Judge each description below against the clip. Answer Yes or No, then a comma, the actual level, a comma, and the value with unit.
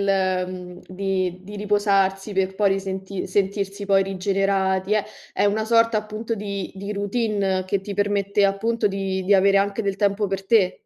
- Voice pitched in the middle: No, high, 195 Hz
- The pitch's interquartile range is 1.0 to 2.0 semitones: Yes, narrow, 1.3 semitones